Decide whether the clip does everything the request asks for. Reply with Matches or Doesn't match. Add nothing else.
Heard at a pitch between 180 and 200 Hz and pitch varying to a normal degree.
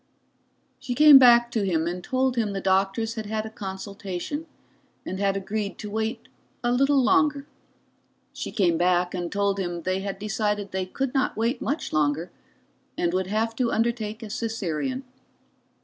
Doesn't match